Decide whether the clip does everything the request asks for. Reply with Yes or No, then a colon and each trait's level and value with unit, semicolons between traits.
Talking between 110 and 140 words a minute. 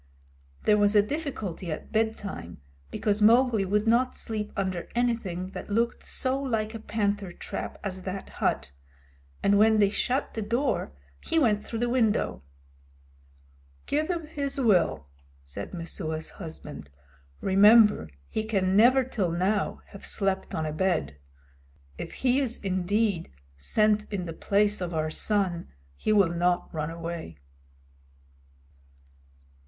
Yes: slow, 135 wpm